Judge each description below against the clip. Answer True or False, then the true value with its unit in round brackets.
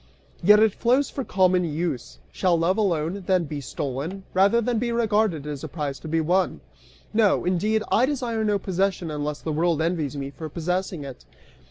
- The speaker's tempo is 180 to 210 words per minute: True (185 wpm)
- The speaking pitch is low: False (180 Hz)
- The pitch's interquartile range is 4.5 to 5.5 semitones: True (5.2 semitones)